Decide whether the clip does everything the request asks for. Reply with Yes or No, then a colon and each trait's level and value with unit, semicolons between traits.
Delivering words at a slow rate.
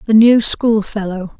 Yes: slow, 130 wpm